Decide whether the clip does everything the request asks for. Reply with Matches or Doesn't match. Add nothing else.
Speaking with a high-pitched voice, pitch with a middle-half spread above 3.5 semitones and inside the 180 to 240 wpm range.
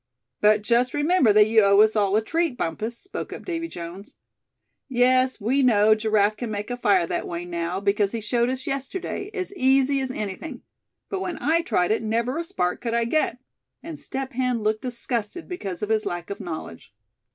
Matches